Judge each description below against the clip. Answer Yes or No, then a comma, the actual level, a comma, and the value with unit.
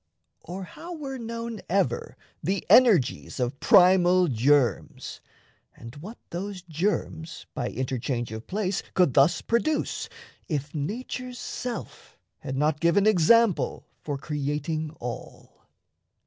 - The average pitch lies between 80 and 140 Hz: No, medium, 175 Hz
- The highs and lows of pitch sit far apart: Yes, wide, 6.7 semitones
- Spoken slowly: Yes, slow, 115 wpm